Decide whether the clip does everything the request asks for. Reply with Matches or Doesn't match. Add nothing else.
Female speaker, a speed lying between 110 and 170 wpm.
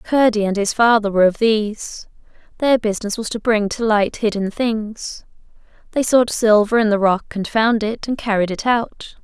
Doesn't match